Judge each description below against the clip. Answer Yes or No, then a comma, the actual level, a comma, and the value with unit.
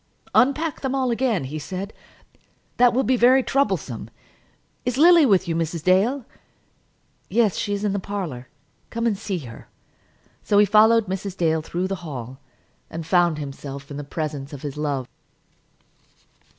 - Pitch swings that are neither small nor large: No, wide, 7.3 semitones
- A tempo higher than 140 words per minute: Yes, average, 160 wpm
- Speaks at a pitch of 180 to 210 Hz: Yes, high, 190 Hz